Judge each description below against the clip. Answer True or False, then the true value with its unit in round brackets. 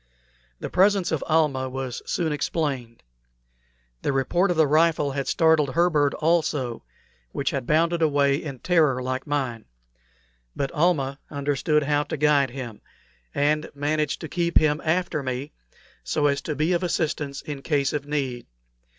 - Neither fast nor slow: True (155 wpm)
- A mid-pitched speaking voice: True (145 Hz)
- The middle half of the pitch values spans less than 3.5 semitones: True (2.8 semitones)